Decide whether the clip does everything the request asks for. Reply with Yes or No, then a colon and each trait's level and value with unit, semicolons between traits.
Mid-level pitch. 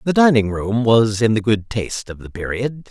No: low, 115 Hz